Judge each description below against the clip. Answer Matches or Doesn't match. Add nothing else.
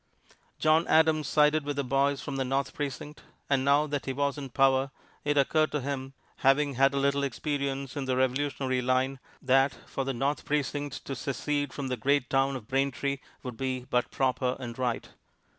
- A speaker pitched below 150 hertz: Matches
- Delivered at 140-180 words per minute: Doesn't match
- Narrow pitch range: Matches